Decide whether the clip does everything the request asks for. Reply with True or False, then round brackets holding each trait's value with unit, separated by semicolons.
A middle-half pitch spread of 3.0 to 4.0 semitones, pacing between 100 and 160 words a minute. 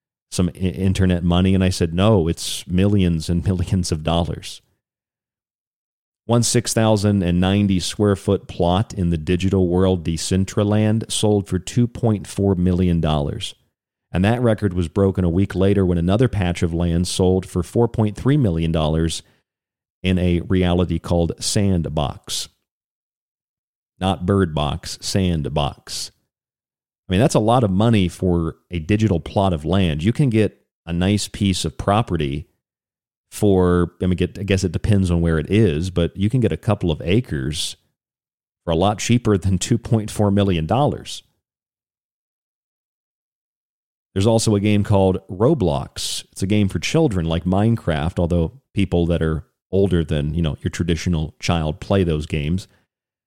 True (3.3 semitones; 145 wpm)